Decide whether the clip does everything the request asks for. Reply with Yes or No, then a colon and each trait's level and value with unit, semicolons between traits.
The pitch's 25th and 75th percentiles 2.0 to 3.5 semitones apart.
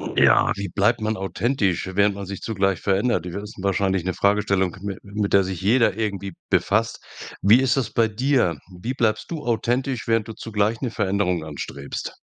Yes: average, 2.9 semitones